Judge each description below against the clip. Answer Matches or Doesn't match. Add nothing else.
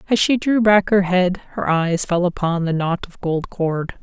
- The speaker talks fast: Matches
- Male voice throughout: Doesn't match